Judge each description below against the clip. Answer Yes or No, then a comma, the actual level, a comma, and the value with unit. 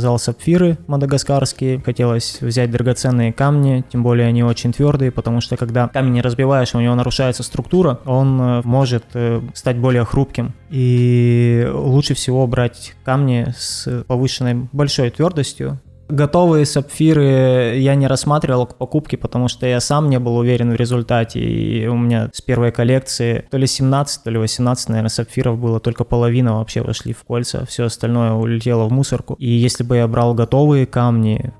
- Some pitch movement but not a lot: No, narrow, 2.0 semitones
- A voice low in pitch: Yes, low, 125 Hz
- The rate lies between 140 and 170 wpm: Yes, fast, 160 wpm